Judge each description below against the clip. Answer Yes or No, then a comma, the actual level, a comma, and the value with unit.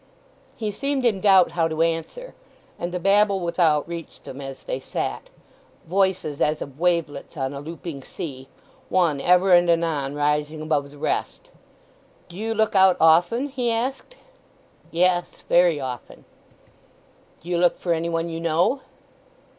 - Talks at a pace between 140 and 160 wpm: Yes, average, 145 wpm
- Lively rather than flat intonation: No, average, 3.8 semitones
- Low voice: No, medium, 170 Hz